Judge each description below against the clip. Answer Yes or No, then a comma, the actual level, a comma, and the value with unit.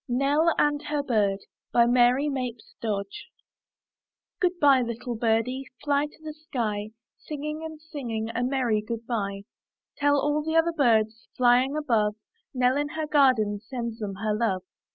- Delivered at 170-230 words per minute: No, average, 150 wpm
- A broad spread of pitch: No, average, 4.7 semitones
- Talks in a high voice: Yes, very high, 250 Hz